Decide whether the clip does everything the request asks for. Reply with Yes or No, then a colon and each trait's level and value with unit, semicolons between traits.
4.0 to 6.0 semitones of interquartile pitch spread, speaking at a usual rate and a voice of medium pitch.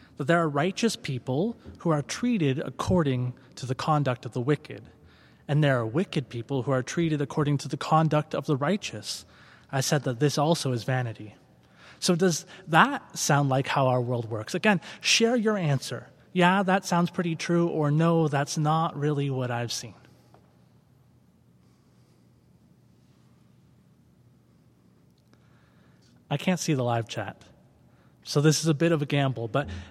Yes: average, 4.6 semitones; average, 155 wpm; medium, 145 Hz